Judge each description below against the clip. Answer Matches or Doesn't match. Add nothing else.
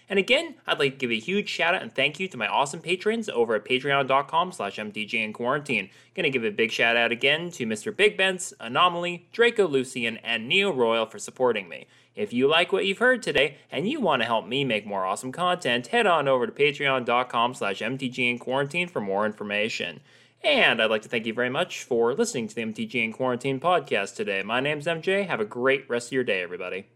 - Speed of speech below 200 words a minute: Doesn't match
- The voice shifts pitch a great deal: Matches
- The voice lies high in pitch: Doesn't match